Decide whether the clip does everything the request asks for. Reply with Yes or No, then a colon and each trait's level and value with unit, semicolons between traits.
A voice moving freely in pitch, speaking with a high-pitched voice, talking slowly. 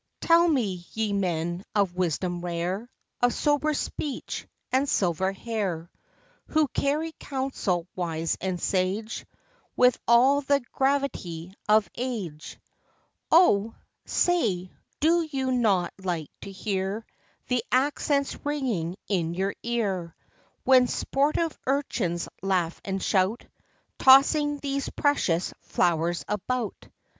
Yes: wide, 7.2 semitones; high, 210 Hz; slow, 120 wpm